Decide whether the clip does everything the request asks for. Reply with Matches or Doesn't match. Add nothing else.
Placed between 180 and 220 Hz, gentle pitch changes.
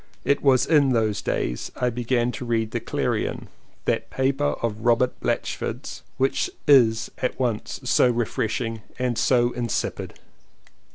Doesn't match